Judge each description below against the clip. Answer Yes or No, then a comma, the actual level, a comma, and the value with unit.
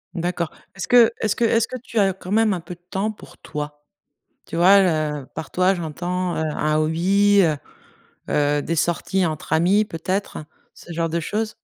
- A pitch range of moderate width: Yes, average, 4.0 semitones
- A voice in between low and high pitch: Yes, medium, 180 Hz